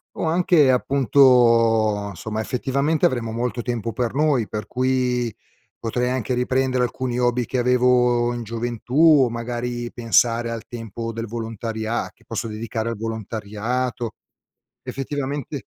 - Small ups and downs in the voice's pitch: Yes, narrow, 1.8 semitones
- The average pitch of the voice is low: Yes, low, 120 Hz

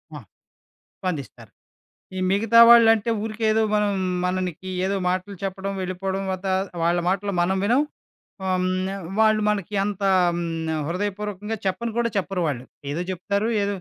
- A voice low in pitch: No, high, 195 Hz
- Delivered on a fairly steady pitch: Yes, narrow, 2.3 semitones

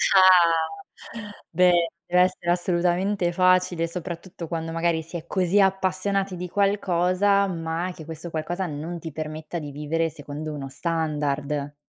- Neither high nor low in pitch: Yes, medium, 170 Hz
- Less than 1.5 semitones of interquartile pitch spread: No, narrow, 2.4 semitones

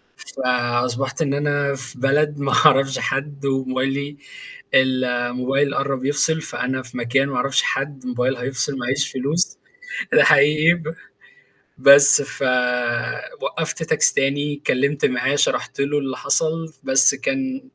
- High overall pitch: No, low, 135 Hz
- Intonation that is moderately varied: No, narrow, 2.1 semitones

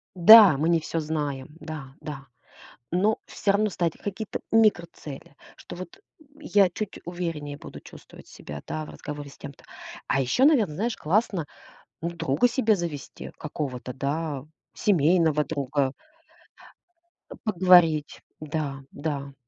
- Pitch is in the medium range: Yes, medium, 160 Hz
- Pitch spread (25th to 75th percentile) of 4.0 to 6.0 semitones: Yes, wide, 5.4 semitones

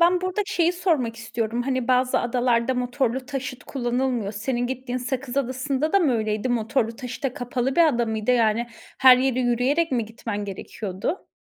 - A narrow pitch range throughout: Yes, narrow, 2.3 semitones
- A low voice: No, very high, 250 Hz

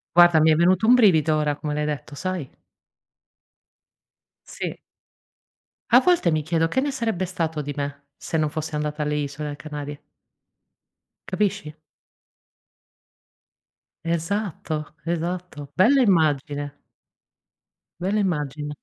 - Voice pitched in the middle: Yes, medium, 160 Hz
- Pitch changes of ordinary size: Yes, average, 3.7 semitones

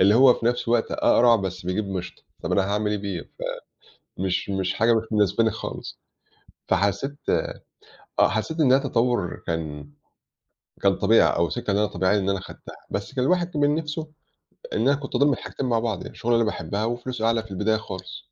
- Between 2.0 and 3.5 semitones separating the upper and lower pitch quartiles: No, average, 4.2 semitones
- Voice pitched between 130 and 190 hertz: No, low, 110 Hz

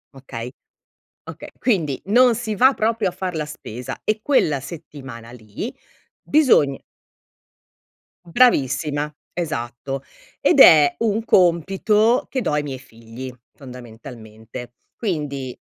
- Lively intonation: Yes, wide, 8.6 semitones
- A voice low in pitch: No, medium, 150 Hz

